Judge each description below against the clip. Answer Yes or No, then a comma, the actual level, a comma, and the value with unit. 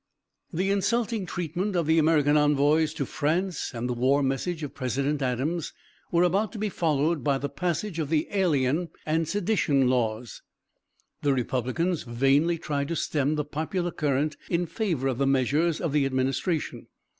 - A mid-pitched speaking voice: Yes, medium, 150 Hz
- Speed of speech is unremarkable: Yes, average, 165 wpm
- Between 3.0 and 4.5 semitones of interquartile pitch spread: Yes, average, 4.1 semitones